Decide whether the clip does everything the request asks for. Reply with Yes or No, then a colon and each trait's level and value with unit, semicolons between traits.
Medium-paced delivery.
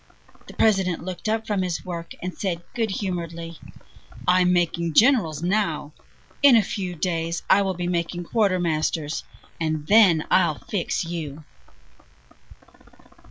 No: slow, 130 wpm